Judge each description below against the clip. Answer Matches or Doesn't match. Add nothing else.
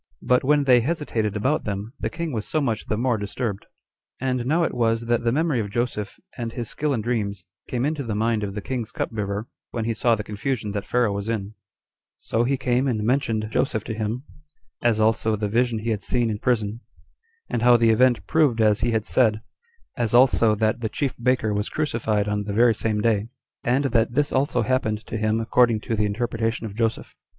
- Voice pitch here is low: Matches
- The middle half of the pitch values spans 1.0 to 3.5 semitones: Matches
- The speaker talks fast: Matches